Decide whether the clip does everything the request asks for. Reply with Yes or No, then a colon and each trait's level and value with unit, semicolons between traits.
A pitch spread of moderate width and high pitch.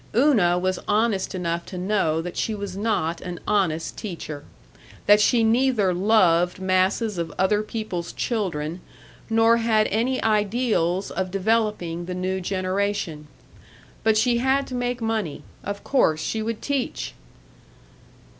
Yes: average, 4.0 semitones; high, 200 Hz